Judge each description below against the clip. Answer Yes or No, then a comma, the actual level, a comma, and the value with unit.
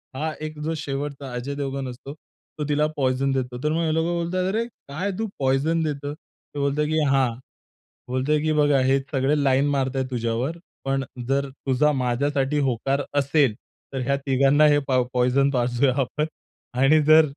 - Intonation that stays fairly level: Yes, narrow, 2.3 semitones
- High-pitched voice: No, medium, 140 Hz